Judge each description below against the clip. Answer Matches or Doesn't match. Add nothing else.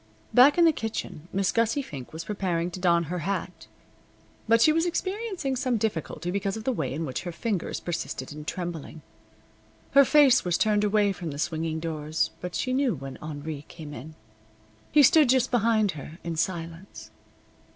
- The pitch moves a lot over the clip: Matches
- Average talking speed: Matches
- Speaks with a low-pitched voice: Doesn't match